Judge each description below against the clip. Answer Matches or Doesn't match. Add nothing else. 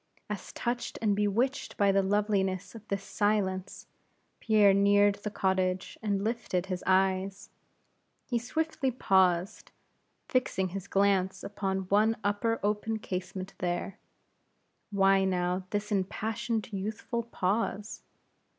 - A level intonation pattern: Matches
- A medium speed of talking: Doesn't match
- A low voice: Doesn't match